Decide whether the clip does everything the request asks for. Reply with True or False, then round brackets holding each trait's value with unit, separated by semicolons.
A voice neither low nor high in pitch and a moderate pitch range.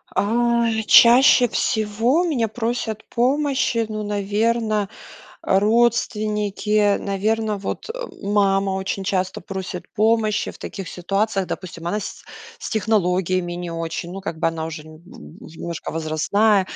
False (205 Hz; 3.3 semitones)